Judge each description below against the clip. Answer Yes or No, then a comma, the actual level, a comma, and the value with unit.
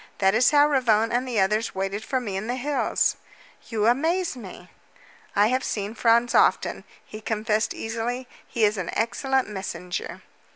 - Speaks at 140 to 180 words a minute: Yes, average, 165 wpm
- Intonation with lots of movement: No, average, 3.2 semitones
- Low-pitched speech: No, high, 225 Hz